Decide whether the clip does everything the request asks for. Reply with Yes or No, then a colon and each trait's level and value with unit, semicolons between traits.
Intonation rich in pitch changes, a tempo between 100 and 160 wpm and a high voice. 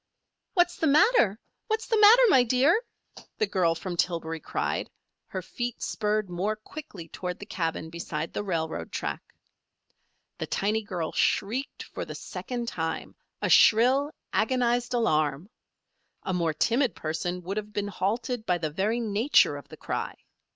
Yes: wide, 6.2 semitones; average, 150 wpm; high, 210 Hz